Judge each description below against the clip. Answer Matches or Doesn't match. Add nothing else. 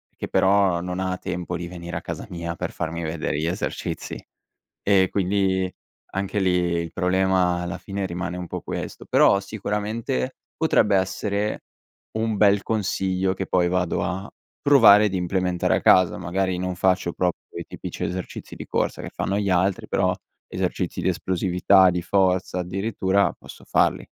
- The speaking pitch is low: Matches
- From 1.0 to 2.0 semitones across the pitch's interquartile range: Matches